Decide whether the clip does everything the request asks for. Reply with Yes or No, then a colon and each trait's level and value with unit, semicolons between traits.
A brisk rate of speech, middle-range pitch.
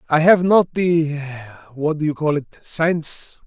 No: average, 140 wpm; medium, 155 Hz